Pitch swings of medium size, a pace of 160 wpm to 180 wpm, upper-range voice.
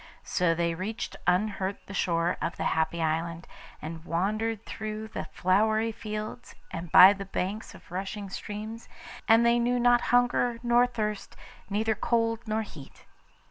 No: average, 4.1 semitones; average, 150 wpm; high, 210 Hz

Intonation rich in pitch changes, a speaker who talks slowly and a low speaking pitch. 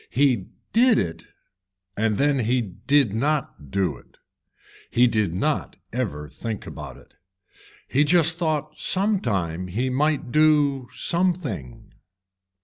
Yes: wide, 7.5 semitones; slow, 125 wpm; low, 130 Hz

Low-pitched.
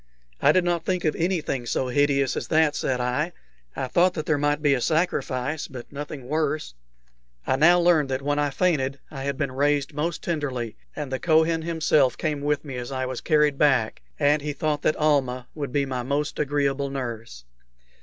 No: medium, 145 Hz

